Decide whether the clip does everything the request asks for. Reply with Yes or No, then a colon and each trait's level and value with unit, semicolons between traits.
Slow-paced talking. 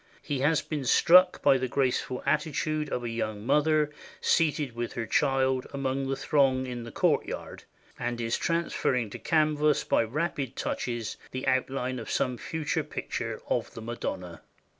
No: average, 160 wpm